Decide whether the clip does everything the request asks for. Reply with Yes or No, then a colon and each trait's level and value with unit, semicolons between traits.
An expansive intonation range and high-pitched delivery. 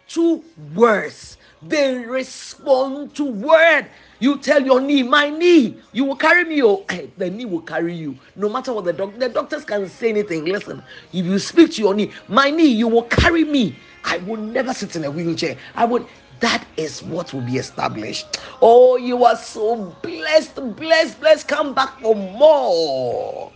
Yes: wide, 6.7 semitones; high, 245 Hz